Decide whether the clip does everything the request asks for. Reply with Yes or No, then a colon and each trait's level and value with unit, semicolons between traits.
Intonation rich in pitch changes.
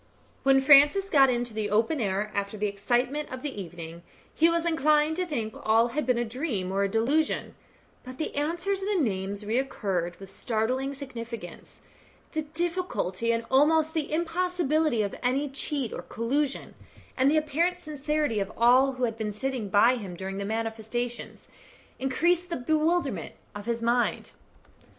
Yes: wide, 5.7 semitones